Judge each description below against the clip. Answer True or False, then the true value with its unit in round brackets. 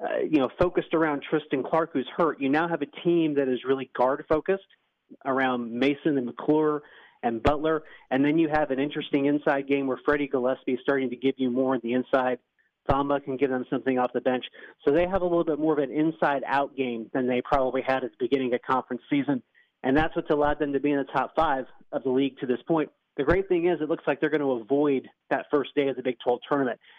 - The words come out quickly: True (245 wpm)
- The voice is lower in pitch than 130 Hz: False (140 Hz)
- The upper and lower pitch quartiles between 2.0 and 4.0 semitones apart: True (3.1 semitones)